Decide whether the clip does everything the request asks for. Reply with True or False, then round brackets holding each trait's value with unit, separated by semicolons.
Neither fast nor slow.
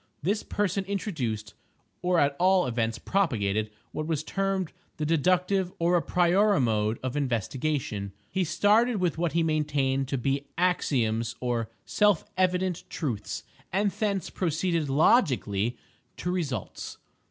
False (130 wpm)